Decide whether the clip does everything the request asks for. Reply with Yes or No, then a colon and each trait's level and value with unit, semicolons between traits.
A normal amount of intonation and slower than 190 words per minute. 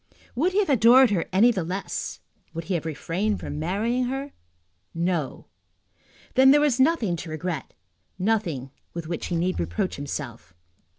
No: wide, 7.0 semitones; average, 160 wpm